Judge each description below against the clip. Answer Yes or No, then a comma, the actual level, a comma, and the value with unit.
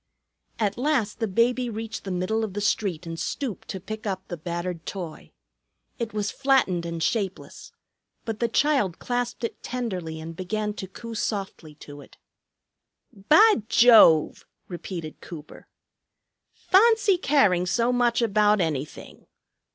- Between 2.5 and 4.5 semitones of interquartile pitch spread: No, average, 5.1 semitones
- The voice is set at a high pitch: Yes, high, 210 Hz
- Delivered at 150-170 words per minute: No, average, 140 wpm